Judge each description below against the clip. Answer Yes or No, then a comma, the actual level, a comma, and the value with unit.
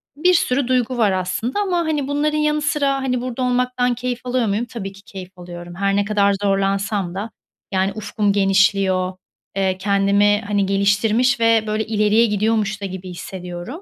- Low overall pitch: No, high, 210 Hz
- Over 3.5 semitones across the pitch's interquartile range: Yes, average, 4.3 semitones